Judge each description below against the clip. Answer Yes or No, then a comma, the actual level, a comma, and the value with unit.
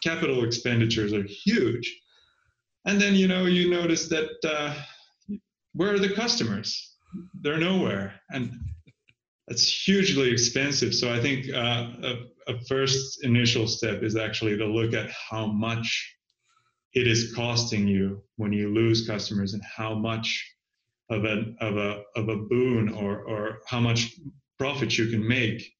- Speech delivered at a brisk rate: No, average, 150 wpm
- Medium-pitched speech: No, low, 120 Hz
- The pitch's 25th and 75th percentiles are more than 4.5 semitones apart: Yes, average, 5.0 semitones